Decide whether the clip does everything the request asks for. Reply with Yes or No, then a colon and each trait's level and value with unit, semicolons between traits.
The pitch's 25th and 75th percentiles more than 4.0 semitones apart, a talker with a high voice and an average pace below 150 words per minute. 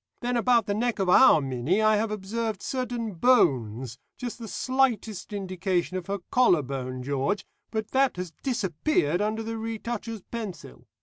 No: average, 5.0 semitones; high, 210 Hz; average, 160 wpm